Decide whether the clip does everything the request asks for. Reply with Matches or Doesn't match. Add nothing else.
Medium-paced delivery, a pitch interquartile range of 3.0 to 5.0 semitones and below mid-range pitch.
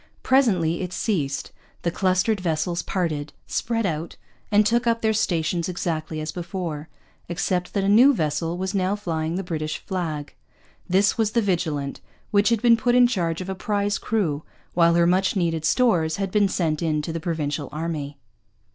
Doesn't match